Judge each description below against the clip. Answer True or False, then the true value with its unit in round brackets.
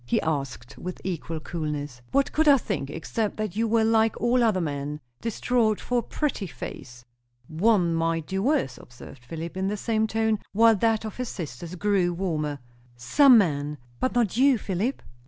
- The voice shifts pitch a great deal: True (6.4 semitones)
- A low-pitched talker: False (190 Hz)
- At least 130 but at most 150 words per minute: False (175 wpm)